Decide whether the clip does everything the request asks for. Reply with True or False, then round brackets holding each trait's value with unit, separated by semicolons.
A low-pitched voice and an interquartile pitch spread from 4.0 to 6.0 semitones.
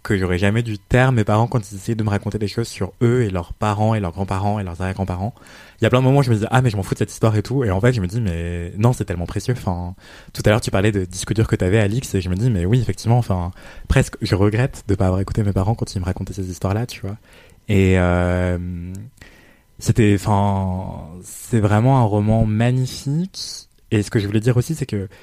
False (105 Hz; 3.6 semitones)